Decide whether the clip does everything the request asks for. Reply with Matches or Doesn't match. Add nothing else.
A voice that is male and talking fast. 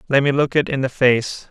Matches